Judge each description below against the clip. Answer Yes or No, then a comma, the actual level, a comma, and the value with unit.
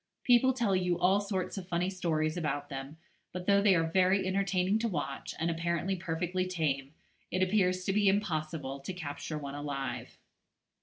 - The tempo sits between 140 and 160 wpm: No, average, 170 wpm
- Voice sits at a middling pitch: Yes, medium, 180 Hz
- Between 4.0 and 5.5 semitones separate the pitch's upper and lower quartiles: No, average, 3.6 semitones